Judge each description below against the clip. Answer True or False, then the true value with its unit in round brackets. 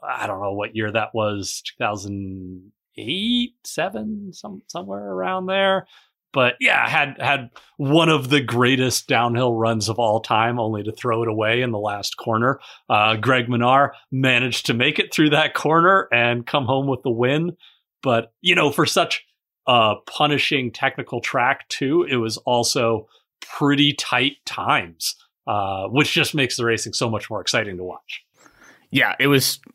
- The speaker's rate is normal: True (170 wpm)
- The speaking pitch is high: False (125 Hz)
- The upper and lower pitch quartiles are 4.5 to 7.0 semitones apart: True (4.8 semitones)